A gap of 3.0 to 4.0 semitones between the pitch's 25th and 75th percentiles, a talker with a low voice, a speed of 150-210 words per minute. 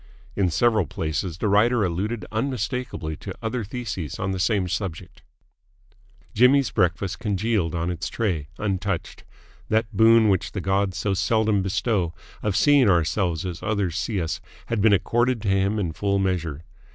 Yes: average, 3.6 semitones; low, 100 Hz; average, 155 wpm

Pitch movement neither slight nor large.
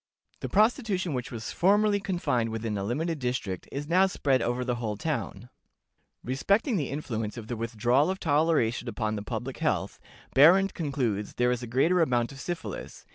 No: wide, 6.8 semitones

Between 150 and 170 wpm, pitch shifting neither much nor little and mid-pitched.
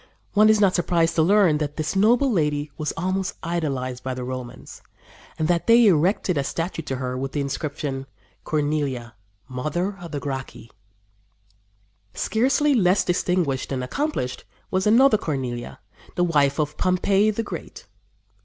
No: average, 155 wpm; wide, 5.9 semitones; medium, 160 Hz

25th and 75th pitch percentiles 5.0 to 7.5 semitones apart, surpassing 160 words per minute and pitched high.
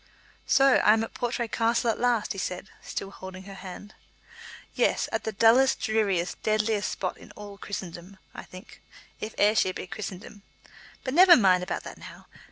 No: average, 3.2 semitones; average, 175 wpm; high, 210 Hz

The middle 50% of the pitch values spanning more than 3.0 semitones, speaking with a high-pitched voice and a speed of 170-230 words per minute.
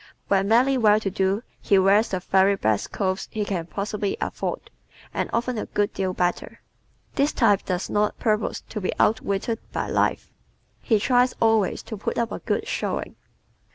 No: average, 2.7 semitones; high, 205 Hz; average, 175 wpm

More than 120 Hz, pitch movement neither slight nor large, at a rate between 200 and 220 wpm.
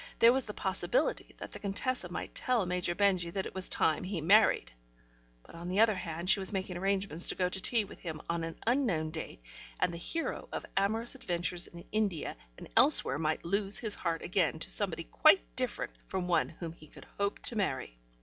Yes: medium, 185 Hz; average, 3.4 semitones; fast, 205 wpm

